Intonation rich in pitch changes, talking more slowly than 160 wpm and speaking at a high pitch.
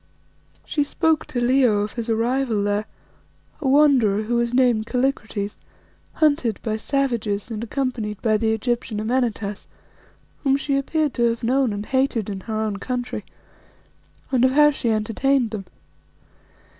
No: average, 3.7 semitones; average, 145 wpm; high, 235 Hz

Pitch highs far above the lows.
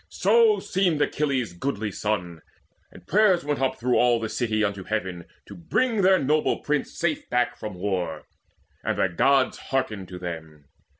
Yes: wide, 7.8 semitones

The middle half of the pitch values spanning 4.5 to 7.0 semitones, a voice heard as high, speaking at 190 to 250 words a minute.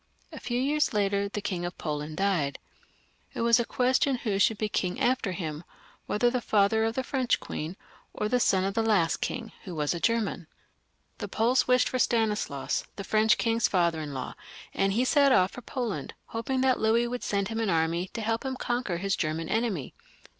Yes: average, 5.0 semitones; high, 215 Hz; fast, 205 wpm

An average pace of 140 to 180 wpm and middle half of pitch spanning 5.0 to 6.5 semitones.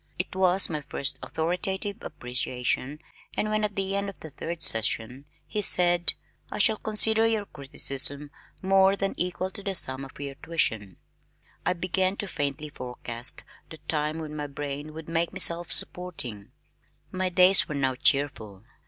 Yes: average, 160 wpm; wide, 5.5 semitones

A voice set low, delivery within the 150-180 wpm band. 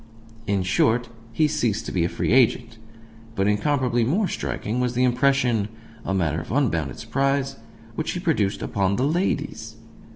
Yes: low, 120 Hz; average, 160 wpm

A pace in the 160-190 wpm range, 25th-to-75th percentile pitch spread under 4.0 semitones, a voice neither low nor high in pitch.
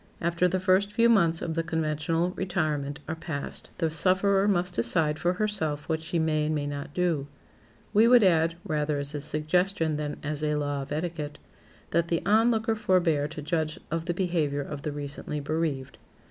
Yes: average, 185 wpm; average, 3.4 semitones; medium, 160 Hz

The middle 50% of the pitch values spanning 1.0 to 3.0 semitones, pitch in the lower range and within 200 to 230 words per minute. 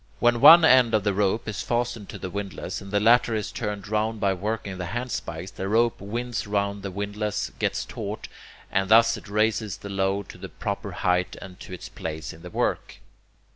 Yes: average, 2.7 semitones; low, 105 Hz; fast, 205 wpm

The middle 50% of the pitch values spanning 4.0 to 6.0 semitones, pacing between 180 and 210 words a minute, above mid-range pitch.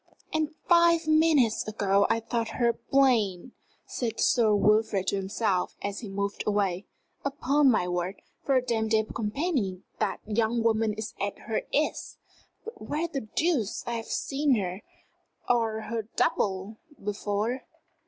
No: average, 4.3 semitones; average, 145 wpm; high, 220 Hz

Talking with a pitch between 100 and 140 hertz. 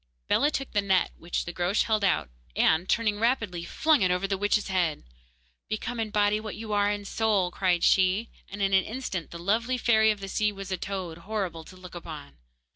No: high, 200 Hz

